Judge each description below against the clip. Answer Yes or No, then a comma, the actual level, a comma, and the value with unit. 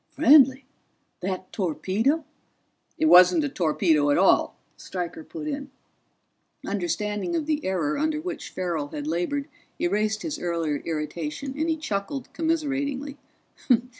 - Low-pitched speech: No, high, 215 Hz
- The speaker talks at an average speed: No, slow, 130 wpm